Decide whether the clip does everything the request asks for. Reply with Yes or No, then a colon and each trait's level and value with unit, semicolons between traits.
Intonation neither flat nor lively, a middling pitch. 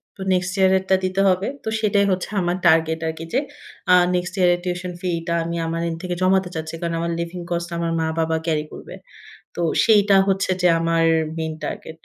No: narrow, 2.1 semitones; medium, 175 Hz